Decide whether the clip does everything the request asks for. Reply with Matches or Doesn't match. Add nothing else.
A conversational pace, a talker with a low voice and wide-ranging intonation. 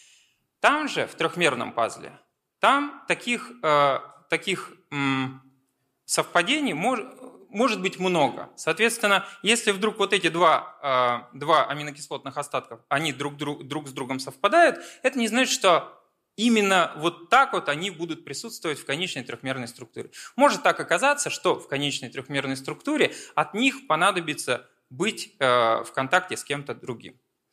Doesn't match